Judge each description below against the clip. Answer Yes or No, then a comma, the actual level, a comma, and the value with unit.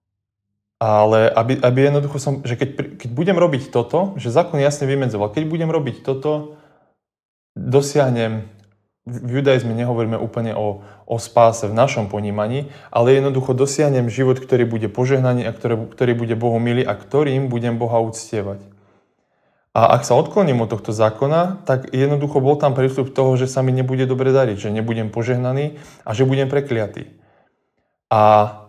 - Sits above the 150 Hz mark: No, low, 125 Hz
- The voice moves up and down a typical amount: Yes, average, 3.5 semitones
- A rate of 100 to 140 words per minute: No, average, 155 wpm